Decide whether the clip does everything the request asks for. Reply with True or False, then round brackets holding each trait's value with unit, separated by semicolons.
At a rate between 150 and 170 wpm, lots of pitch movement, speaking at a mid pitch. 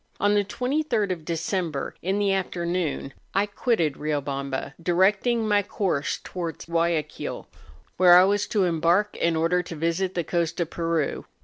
False (155 wpm; 3.4 semitones; 175 Hz)